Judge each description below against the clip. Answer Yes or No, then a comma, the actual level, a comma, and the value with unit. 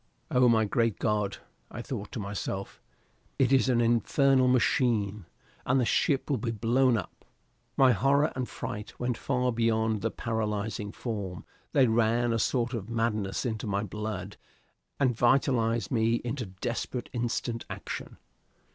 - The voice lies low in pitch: Yes, low, 115 Hz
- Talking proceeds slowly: No, average, 145 wpm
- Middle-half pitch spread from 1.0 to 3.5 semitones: Yes, average, 2.9 semitones